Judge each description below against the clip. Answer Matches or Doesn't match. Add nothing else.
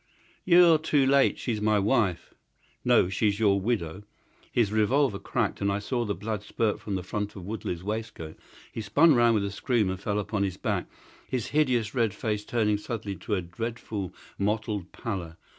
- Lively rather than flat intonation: Doesn't match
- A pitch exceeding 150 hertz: Doesn't match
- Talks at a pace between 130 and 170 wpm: Doesn't match